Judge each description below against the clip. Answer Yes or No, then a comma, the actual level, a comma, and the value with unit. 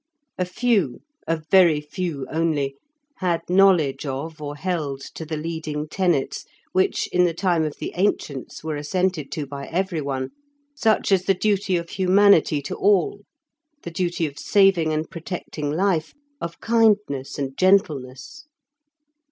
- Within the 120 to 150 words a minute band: Yes, average, 145 wpm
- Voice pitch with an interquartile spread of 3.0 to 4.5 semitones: Yes, average, 4.2 semitones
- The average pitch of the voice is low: No, medium, 165 Hz